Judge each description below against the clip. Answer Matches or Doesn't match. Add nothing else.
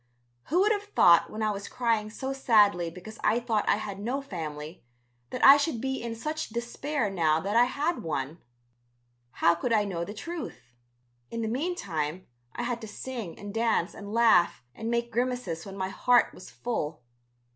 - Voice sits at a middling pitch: Doesn't match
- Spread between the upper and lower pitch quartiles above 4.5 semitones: Matches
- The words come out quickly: Doesn't match